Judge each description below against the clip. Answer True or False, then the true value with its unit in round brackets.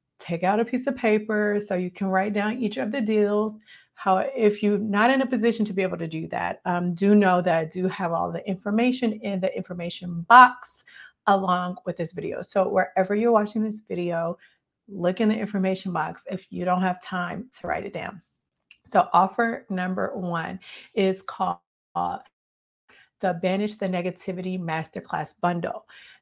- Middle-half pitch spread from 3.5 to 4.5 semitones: False (3.0 semitones)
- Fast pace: False (180 wpm)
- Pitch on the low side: False (190 Hz)